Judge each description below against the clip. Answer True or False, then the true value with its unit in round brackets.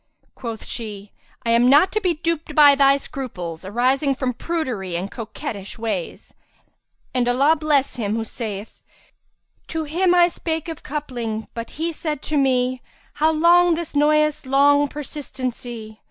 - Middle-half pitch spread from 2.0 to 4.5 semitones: False (4.9 semitones)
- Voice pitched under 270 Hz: False (275 Hz)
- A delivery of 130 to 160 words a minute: True (155 wpm)